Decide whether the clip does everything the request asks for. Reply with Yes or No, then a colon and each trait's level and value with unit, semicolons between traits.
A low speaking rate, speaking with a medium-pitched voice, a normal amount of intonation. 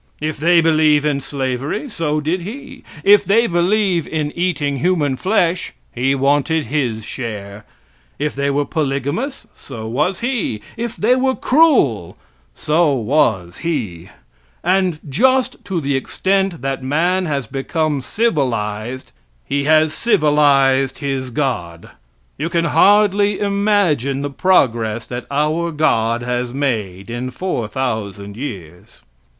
No: slow, 130 wpm; medium, 145 Hz; wide, 6.0 semitones